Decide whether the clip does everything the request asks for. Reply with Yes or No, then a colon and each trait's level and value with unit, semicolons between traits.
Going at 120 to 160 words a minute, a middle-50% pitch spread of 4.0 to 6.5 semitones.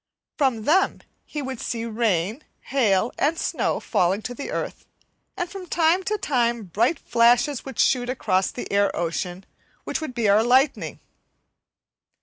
Yes: average, 150 wpm; average, 5.3 semitones